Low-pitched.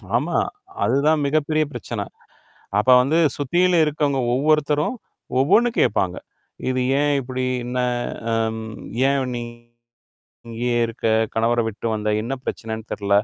Yes: low, 130 Hz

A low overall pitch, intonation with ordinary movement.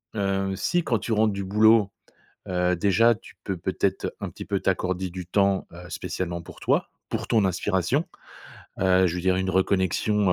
No: very low, 95 Hz; narrow, 2.2 semitones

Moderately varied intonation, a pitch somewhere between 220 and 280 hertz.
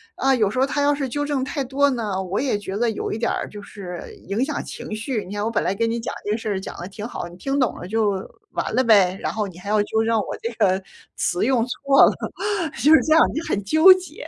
Yes: average, 4.8 semitones; high, 225 Hz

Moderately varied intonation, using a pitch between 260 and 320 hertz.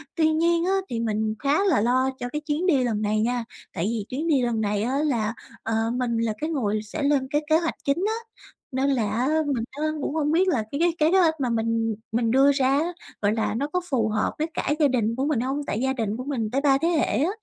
Yes: average, 5.0 semitones; very high, 265 Hz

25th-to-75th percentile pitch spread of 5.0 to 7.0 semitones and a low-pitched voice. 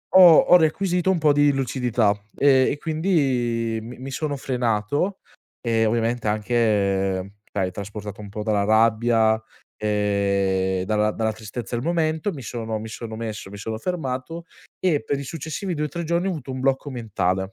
Yes: wide, 5.5 semitones; low, 120 Hz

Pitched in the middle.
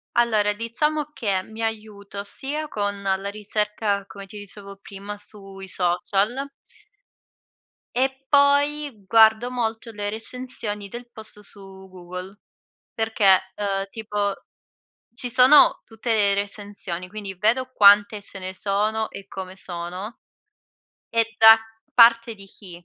No: high, 210 Hz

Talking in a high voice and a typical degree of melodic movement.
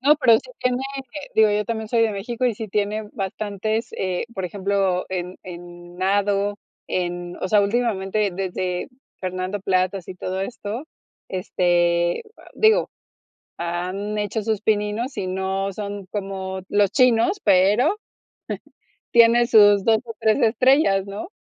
Yes: high, 200 Hz; average, 3.1 semitones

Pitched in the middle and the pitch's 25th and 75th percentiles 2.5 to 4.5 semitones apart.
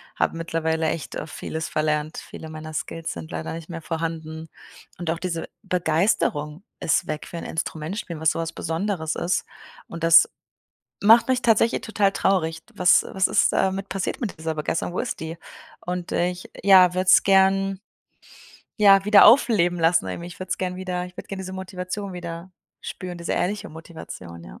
Yes: medium, 175 Hz; average, 2.9 semitones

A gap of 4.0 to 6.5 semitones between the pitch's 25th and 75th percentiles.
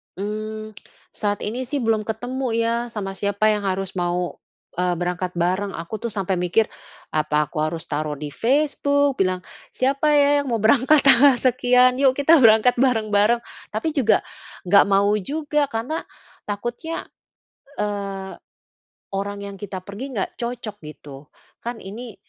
Yes: average, 4.5 semitones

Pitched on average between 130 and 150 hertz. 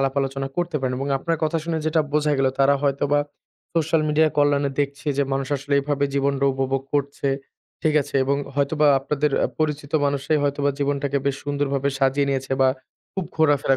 Yes: medium, 140 Hz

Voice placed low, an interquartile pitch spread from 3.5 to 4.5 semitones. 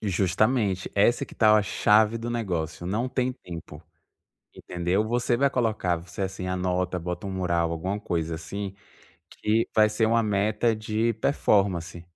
Yes: low, 100 Hz; average, 3.8 semitones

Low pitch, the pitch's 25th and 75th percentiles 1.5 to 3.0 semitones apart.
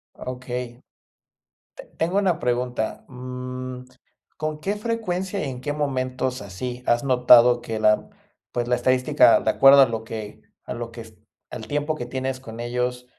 Yes: low, 125 Hz; narrow, 2.5 semitones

